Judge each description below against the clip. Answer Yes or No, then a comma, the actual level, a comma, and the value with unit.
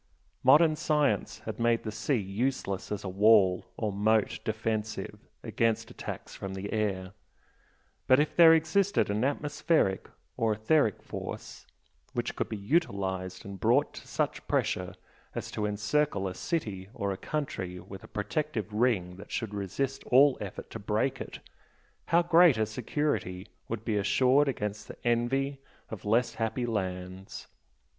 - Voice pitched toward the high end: No, low, 110 Hz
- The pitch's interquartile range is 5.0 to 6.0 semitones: Yes, wide, 5.4 semitones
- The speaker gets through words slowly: No, average, 150 wpm